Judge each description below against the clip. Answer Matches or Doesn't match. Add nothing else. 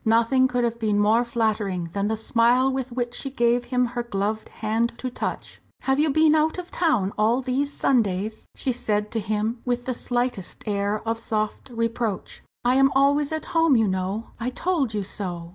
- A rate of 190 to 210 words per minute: Matches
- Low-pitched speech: Doesn't match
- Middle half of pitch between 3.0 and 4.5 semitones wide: Matches